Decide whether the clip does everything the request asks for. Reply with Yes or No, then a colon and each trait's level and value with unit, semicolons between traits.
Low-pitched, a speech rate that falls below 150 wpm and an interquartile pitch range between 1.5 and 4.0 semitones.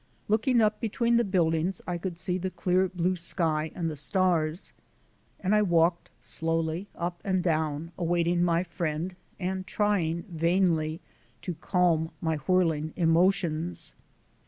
No: medium, 175 Hz; slow, 135 wpm; narrow, 2.4 semitones